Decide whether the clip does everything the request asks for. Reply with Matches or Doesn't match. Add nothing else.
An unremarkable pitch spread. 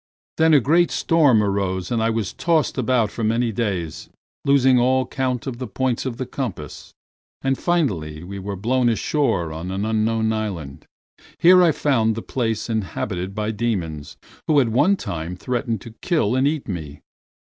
Matches